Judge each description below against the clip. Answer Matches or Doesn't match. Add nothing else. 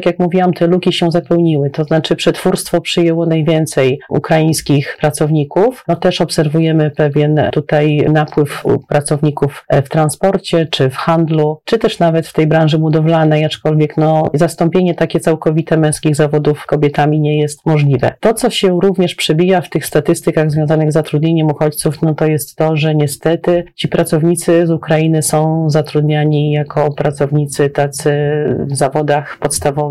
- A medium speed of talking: Matches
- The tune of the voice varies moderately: Doesn't match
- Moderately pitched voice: Matches